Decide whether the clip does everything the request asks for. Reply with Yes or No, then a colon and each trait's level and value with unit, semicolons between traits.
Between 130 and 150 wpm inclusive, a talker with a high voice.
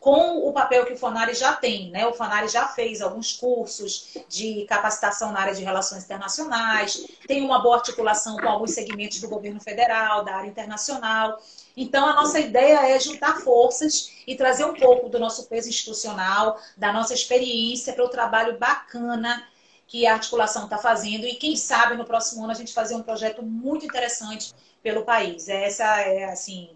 No: average, 180 wpm; high, 230 Hz